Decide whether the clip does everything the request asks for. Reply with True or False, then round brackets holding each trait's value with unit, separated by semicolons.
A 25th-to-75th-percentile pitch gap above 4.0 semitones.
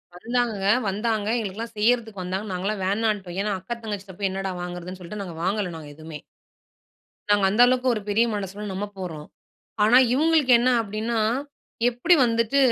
False (3.5 semitones)